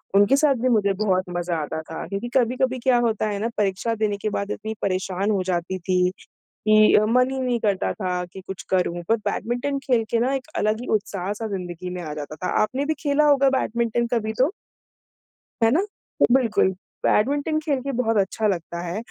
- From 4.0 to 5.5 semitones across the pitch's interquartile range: Yes, average, 5.1 semitones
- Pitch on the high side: Yes, high, 215 Hz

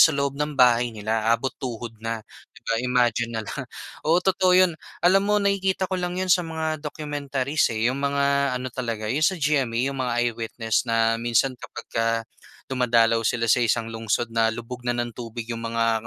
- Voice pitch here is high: No, low, 125 Hz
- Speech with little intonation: No, average, 4.2 semitones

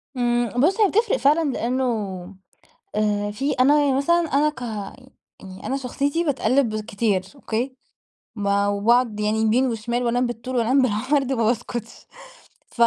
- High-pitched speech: Yes, high, 245 Hz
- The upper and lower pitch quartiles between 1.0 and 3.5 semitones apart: No, average, 4.0 semitones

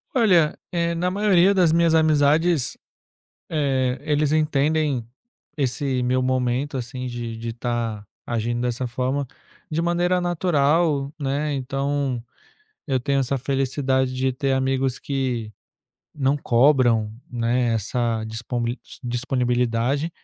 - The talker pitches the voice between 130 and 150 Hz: Yes, low, 135 Hz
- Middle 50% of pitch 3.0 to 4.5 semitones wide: Yes, average, 3.7 semitones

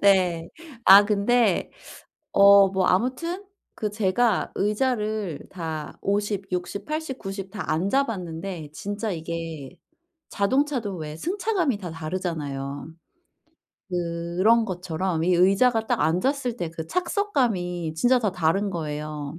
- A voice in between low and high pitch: No, high, 195 Hz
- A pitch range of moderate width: Yes, average, 5.0 semitones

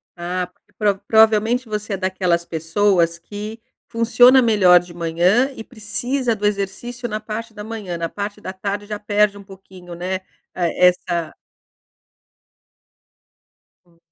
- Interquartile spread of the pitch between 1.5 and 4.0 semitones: Yes, average, 3.5 semitones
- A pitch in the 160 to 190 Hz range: No, high, 205 Hz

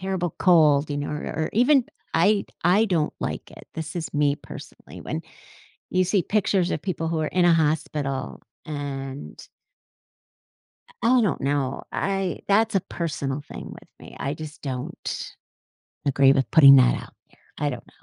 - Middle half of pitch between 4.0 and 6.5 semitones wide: Yes, average, 4.7 semitones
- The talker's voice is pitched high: No, medium, 155 Hz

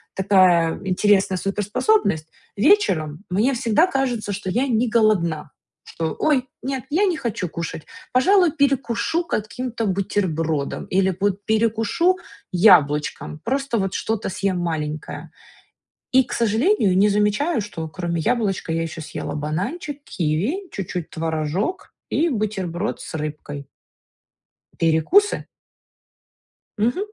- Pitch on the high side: Yes, high, 205 Hz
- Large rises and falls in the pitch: Yes, wide, 7.1 semitones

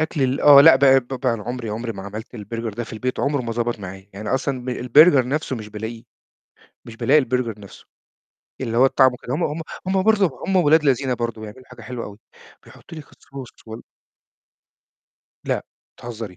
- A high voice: No, low, 125 Hz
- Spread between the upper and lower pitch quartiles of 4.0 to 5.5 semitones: No, average, 3.5 semitones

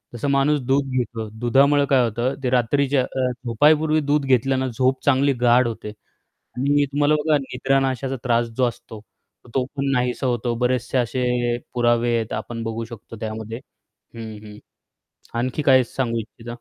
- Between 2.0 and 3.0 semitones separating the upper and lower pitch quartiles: Yes, narrow, 2.5 semitones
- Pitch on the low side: Yes, low, 125 Hz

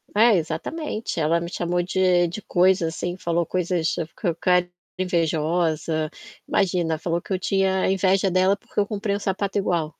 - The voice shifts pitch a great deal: No, narrow, 2.4 semitones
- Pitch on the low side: No, medium, 180 Hz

